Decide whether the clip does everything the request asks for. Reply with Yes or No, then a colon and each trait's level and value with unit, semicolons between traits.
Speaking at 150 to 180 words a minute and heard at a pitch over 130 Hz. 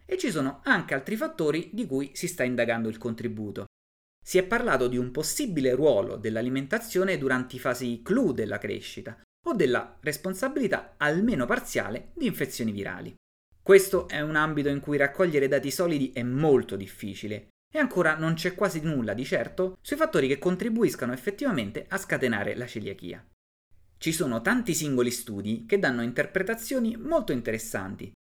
Yes: average, 155 wpm; medium, 140 Hz